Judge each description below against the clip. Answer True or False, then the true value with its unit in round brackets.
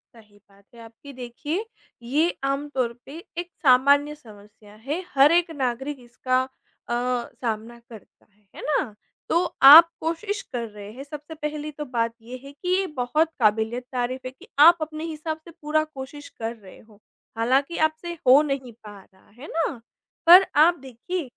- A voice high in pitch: True (270 Hz)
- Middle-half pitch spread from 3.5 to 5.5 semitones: True (4.7 semitones)